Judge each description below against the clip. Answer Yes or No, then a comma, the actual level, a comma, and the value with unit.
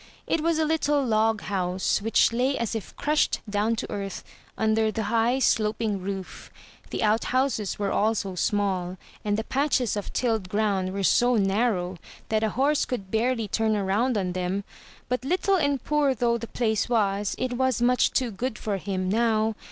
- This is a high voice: Yes, high, 220 Hz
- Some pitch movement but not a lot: Yes, average, 3.7 semitones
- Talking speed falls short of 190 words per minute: Yes, average, 175 wpm